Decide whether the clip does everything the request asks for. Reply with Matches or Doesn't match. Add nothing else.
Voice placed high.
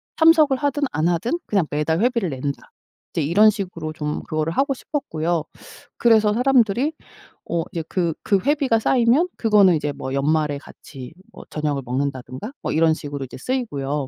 Doesn't match